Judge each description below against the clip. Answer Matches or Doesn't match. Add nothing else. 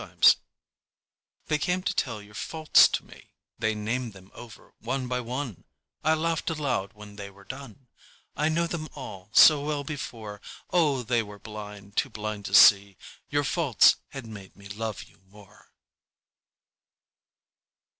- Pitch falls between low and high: Doesn't match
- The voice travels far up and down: Matches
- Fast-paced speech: Doesn't match